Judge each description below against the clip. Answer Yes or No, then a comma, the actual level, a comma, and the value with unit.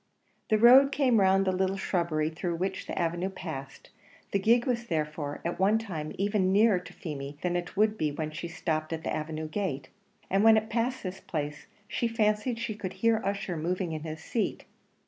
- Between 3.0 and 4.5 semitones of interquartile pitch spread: No, average, 5.3 semitones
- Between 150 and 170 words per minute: No, average, 200 wpm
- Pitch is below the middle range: No, medium, 185 Hz